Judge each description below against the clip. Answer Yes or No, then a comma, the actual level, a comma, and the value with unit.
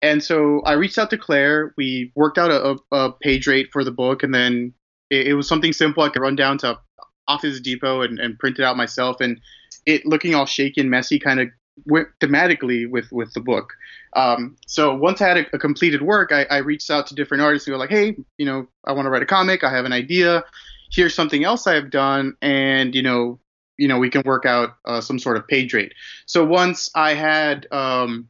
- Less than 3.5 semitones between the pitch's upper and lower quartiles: Yes, average, 3.0 semitones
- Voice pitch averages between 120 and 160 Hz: Yes, medium, 140 Hz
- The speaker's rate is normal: No, fast, 230 wpm